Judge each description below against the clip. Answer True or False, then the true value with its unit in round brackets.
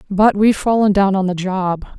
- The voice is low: False (195 Hz)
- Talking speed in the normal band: False (210 wpm)